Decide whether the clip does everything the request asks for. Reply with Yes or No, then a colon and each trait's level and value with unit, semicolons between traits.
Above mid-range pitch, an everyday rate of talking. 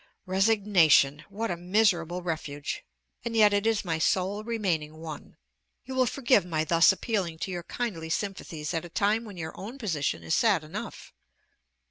No: medium, 180 Hz; average, 165 wpm